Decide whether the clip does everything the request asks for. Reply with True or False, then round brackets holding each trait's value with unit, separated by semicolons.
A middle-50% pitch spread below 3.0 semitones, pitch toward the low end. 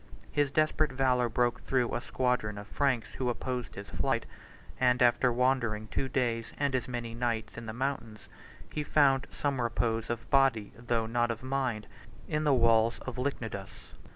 True (2.5 semitones; 120 Hz)